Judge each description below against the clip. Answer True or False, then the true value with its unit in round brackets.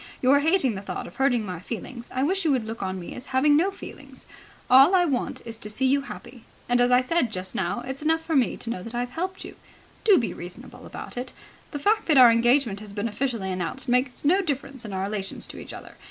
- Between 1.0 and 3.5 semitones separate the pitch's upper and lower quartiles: False (4.7 semitones)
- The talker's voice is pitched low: False (250 Hz)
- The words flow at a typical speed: False (245 wpm)